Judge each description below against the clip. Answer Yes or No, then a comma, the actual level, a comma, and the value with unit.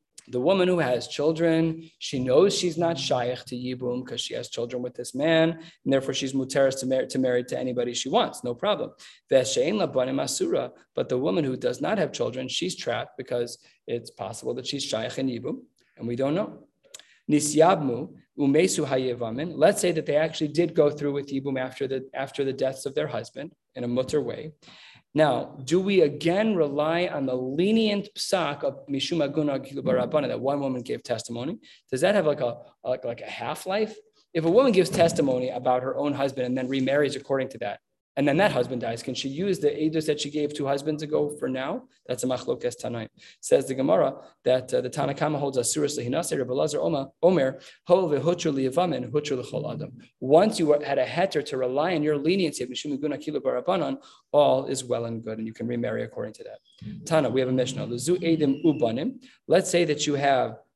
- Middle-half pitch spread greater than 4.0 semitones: Yes, average, 4.6 semitones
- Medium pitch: Yes, medium, 145 Hz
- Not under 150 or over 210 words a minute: Yes, average, 180 wpm